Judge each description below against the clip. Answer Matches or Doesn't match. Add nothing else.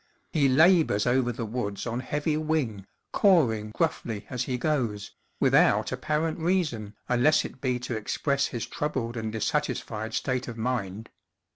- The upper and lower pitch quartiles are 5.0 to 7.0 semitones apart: Matches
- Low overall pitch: Matches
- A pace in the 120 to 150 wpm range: Matches